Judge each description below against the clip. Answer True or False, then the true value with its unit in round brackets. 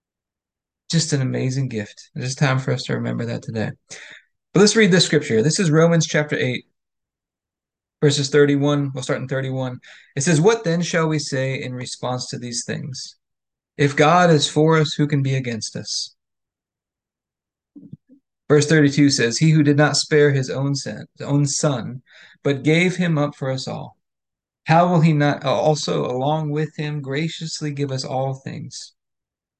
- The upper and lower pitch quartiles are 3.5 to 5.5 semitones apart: False (2.9 semitones)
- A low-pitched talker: False (145 Hz)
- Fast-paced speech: False (165 wpm)